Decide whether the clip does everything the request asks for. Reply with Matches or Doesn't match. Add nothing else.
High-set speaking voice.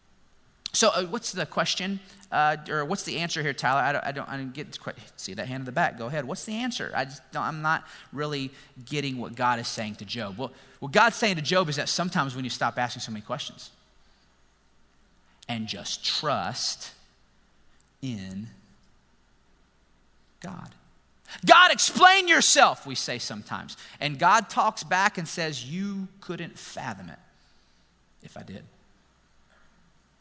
Doesn't match